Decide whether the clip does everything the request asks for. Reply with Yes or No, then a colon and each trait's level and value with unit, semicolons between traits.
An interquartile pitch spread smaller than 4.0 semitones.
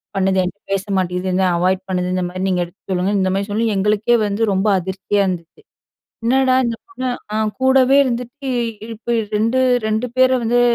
No: average, 4.3 semitones